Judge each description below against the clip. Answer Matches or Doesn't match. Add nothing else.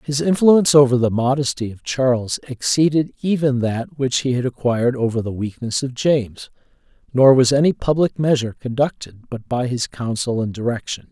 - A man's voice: Matches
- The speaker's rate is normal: Matches